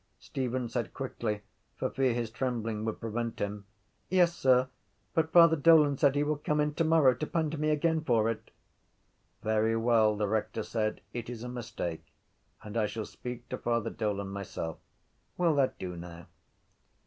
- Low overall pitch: Yes, low, 120 Hz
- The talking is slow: No, average, 170 wpm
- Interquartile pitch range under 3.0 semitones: No, average, 5.2 semitones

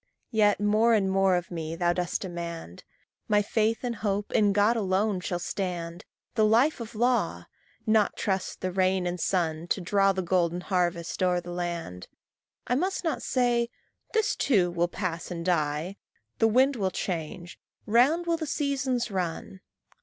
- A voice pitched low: No, high, 190 Hz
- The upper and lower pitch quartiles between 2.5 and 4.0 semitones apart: No, average, 4.4 semitones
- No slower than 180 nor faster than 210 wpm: No, average, 165 wpm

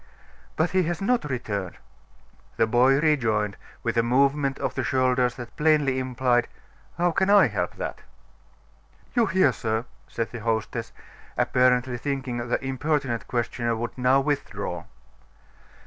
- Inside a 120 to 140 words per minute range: Yes, slow, 135 wpm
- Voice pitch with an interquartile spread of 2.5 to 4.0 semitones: Yes, average, 3.6 semitones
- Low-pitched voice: Yes, low, 130 Hz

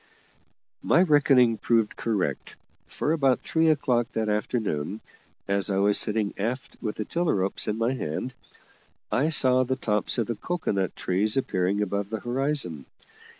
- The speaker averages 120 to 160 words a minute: Yes, average, 155 wpm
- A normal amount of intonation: Yes, average, 4.5 semitones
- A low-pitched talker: Yes, low, 115 Hz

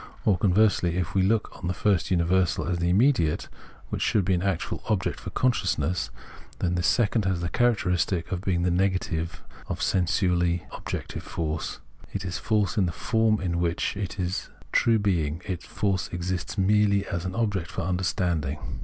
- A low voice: Yes, very low, 90 Hz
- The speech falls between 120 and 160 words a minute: No, average, 170 wpm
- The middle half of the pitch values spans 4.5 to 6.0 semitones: No, narrow, 2.6 semitones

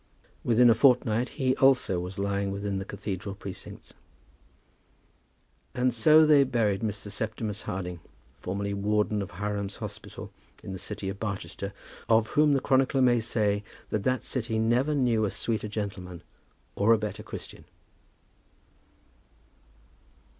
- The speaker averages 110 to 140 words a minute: Yes, slow, 135 wpm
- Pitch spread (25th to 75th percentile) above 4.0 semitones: No, average, 3.6 semitones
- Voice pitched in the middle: No, low, 105 Hz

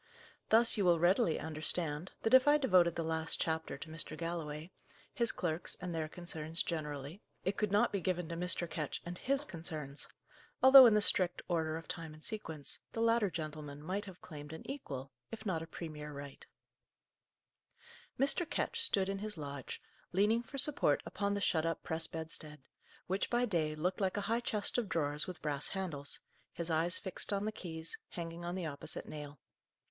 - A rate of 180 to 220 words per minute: Yes, average, 185 wpm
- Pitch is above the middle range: No, medium, 170 Hz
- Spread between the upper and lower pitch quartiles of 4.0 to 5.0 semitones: Yes, average, 4.5 semitones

